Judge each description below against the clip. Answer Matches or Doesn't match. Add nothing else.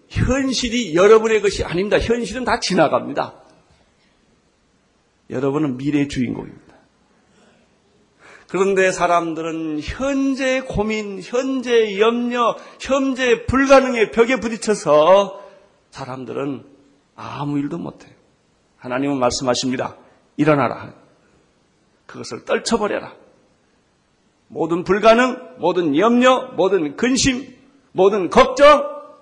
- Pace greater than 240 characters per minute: Doesn't match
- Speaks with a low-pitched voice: Doesn't match